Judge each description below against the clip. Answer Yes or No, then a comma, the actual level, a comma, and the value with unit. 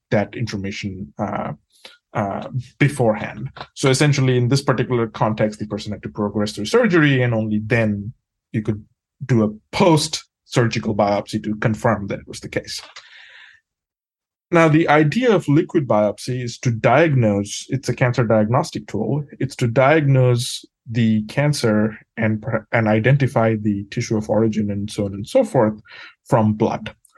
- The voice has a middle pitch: No, low, 115 Hz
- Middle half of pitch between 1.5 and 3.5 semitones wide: No, average, 3.9 semitones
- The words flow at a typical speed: Yes, average, 150 wpm